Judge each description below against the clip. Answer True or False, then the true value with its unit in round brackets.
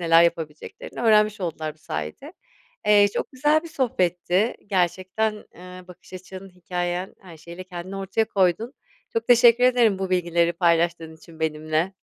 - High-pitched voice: False (180 Hz)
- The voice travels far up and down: False (3.8 semitones)